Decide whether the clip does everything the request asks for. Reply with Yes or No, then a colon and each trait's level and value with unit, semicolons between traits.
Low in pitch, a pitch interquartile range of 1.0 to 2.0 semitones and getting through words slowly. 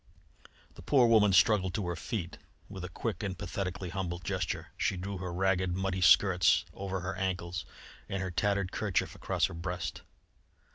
No: very low, 95 Hz; narrow, 1.7 semitones; average, 165 wpm